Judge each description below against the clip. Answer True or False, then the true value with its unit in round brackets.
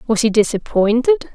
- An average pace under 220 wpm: True (135 wpm)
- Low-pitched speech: False (235 Hz)